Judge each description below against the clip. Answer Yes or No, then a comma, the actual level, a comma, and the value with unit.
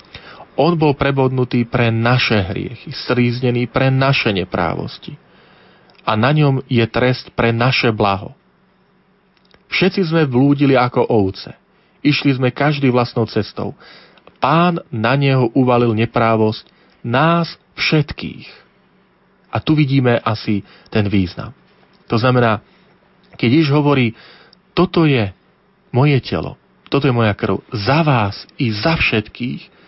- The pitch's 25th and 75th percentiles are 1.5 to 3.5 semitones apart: No, average, 4.8 semitones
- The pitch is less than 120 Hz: No, low, 130 Hz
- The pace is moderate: Yes, average, 120 wpm